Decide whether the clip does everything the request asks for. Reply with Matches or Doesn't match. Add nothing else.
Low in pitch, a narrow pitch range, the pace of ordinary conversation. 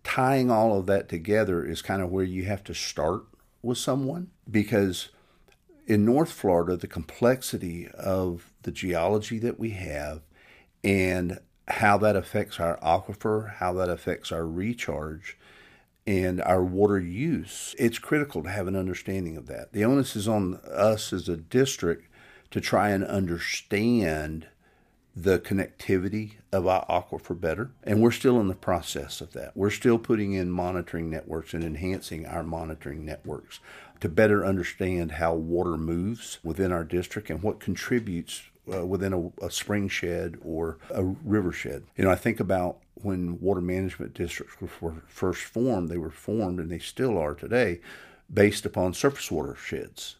Doesn't match